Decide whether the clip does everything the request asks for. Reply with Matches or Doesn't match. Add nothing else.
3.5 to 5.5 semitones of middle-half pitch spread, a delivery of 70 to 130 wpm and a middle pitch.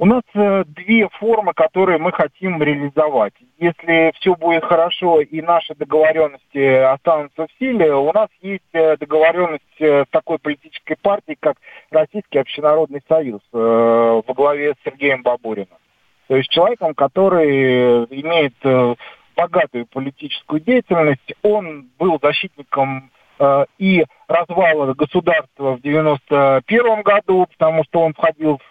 Matches